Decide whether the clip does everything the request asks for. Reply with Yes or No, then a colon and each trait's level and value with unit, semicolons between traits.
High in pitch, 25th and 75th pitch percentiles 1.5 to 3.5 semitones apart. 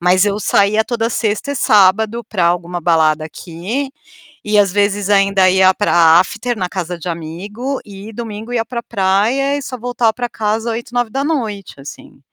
No: high, 205 Hz; average, 4.2 semitones